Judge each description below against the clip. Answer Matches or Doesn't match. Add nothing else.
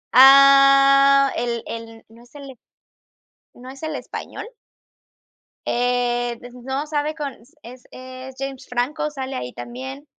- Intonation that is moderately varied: Doesn't match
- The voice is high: Matches